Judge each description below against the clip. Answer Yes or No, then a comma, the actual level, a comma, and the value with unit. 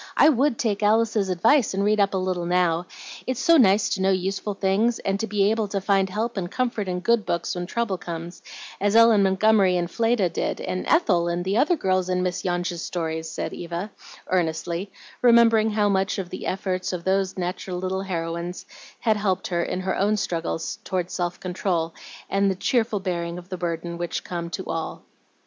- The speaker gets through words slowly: No, average, 195 wpm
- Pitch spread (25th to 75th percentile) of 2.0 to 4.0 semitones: Yes, average, 3.0 semitones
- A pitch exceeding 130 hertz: Yes, high, 190 Hz